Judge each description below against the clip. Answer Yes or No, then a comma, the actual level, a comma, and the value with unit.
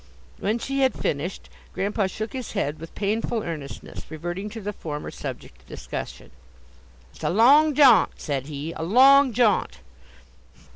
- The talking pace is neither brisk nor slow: Yes, average, 150 wpm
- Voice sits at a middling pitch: No, high, 205 Hz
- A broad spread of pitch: Yes, wide, 6.9 semitones